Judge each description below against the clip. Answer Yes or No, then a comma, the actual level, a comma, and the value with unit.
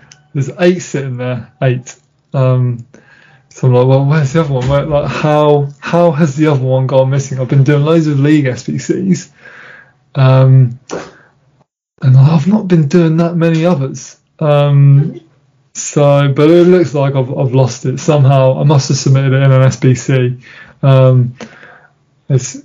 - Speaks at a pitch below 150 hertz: Yes, medium, 140 Hz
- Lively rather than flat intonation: No, average, 2.7 semitones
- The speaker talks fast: No, average, 160 wpm